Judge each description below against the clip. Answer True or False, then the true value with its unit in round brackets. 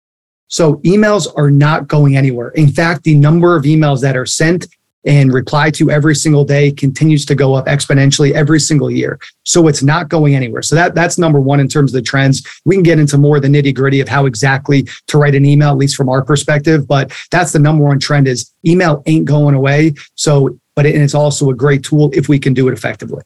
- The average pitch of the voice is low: False (145 Hz)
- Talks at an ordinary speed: False (230 wpm)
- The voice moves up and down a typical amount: False (2.1 semitones)